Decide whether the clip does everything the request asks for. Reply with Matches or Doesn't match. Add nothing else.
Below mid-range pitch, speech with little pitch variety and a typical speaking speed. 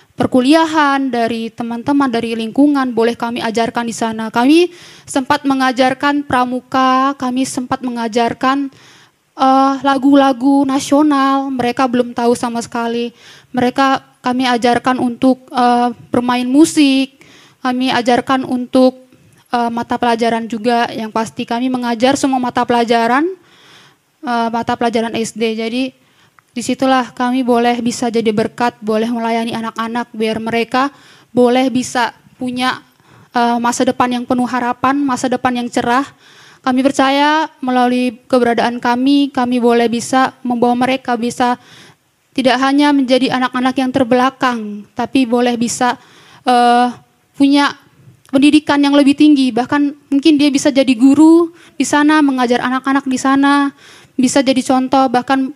Doesn't match